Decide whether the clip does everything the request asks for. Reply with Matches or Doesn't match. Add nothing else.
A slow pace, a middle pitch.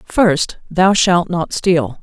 Doesn't match